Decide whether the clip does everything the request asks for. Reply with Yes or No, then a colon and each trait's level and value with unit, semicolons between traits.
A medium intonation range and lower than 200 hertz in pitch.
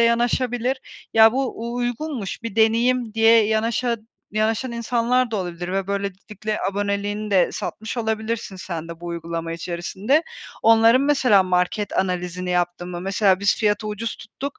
No: average, 3.8 semitones; high, 215 Hz